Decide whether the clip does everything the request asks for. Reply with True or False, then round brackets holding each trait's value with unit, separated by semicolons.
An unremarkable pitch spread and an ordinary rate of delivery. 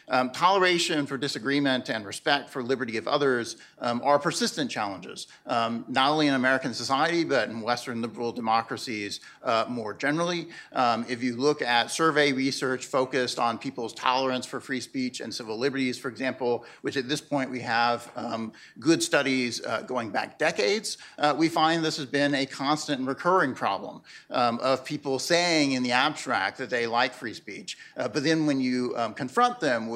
True (3.4 semitones; 185 wpm)